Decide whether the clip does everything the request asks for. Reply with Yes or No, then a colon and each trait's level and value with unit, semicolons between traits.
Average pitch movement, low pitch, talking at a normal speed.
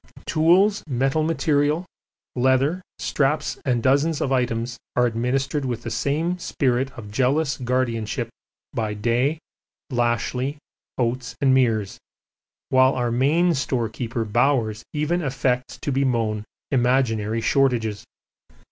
No: average, 3.3 semitones; low, 130 Hz; slow, 110 wpm